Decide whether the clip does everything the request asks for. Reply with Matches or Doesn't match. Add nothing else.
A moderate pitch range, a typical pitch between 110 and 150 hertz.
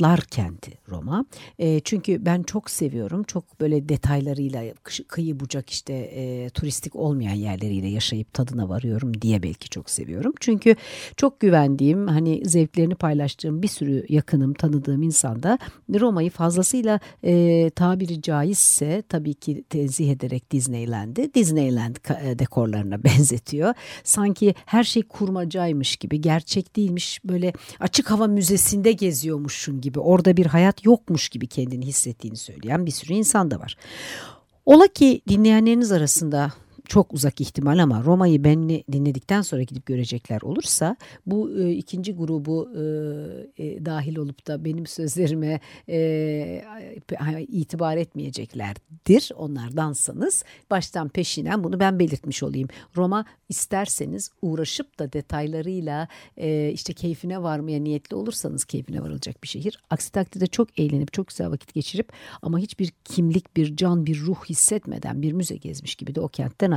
Doesn't match